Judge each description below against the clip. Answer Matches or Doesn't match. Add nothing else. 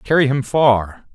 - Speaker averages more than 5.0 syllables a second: Doesn't match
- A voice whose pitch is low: Matches